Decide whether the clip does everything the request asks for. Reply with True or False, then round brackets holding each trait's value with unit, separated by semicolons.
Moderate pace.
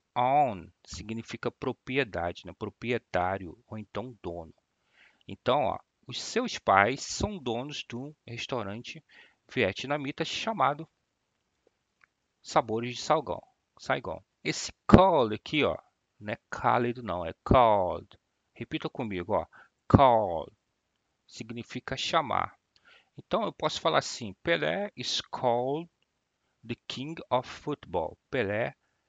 False (105 wpm)